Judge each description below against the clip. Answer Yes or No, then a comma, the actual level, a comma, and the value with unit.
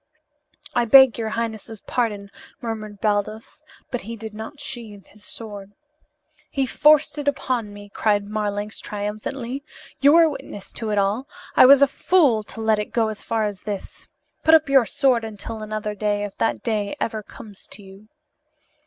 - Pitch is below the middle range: No, high, 220 Hz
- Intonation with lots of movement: No, average, 3.0 semitones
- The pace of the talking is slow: No, average, 170 wpm